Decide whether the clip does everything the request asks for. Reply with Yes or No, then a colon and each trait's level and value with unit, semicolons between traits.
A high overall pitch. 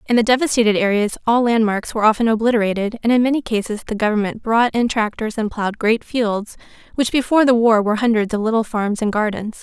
Yes: high, 220 Hz